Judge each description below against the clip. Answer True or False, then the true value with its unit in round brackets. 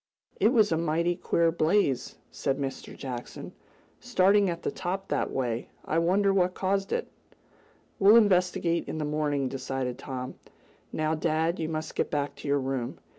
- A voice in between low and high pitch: True (160 Hz)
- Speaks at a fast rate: False (165 wpm)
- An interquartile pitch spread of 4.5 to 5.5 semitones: True (4.9 semitones)